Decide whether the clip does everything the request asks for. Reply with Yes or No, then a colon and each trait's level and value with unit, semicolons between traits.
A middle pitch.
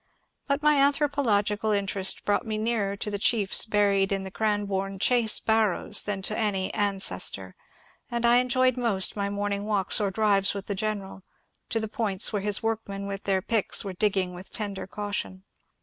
No: high, 205 Hz